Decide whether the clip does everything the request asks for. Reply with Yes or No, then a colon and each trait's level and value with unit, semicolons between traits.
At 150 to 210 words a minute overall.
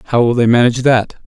No: fast, 235 wpm